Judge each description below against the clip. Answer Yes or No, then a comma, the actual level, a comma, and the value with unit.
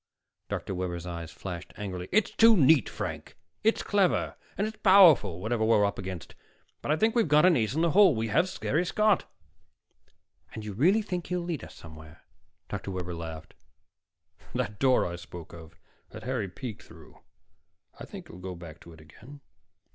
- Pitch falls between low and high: No, low, 110 Hz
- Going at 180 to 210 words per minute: Yes, average, 185 wpm